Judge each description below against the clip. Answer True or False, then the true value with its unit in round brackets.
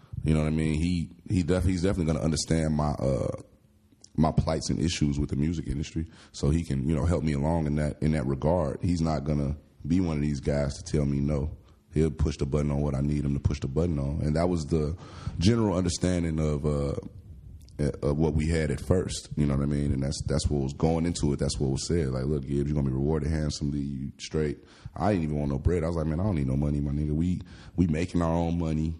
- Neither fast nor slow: False (255 wpm)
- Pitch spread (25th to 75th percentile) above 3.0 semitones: False (2.5 semitones)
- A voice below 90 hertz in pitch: True (75 Hz)